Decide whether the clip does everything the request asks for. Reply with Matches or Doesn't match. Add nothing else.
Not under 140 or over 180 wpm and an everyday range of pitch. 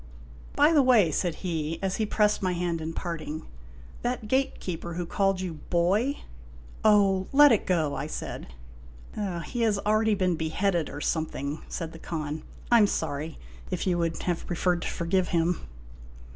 Doesn't match